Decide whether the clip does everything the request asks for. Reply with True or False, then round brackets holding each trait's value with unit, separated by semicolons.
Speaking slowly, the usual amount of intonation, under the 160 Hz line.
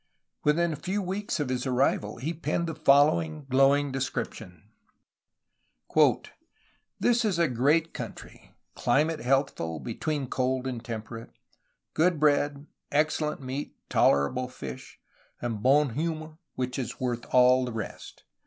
True (130 wpm; 3.8 semitones; 140 Hz)